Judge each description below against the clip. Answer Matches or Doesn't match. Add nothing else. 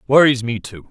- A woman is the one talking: Doesn't match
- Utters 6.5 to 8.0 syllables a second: Doesn't match